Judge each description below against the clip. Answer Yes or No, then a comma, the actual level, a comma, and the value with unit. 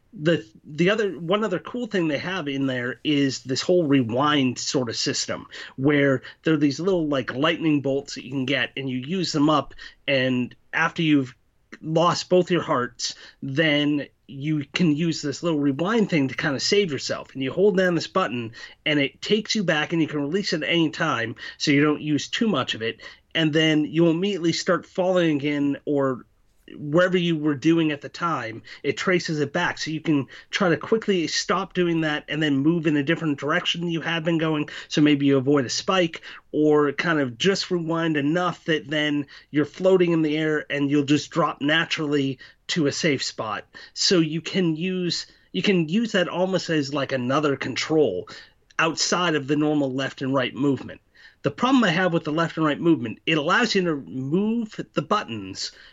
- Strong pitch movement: No, average, 3.6 semitones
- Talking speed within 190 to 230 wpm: Yes, average, 200 wpm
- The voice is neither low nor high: Yes, medium, 155 Hz